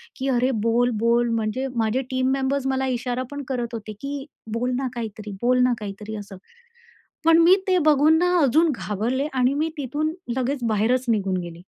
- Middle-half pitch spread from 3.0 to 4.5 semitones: Yes, average, 3.7 semitones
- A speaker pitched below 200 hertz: No, very high, 250 Hz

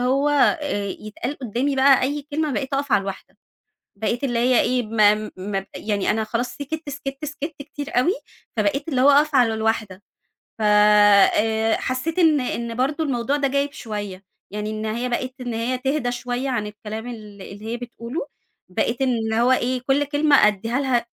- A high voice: Yes, high, 245 Hz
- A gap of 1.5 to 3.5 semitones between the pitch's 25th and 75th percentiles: No, average, 4.3 semitones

